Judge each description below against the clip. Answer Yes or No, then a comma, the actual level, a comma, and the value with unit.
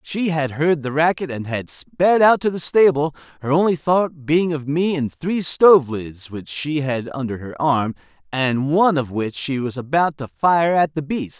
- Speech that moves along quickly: Yes, fast, 210 wpm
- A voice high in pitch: No, medium, 150 Hz